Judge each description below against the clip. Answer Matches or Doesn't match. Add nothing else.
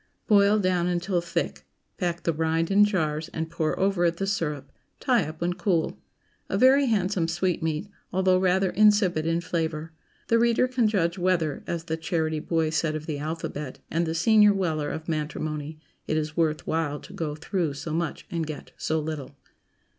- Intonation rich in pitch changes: Doesn't match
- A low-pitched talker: Doesn't match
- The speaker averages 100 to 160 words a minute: Doesn't match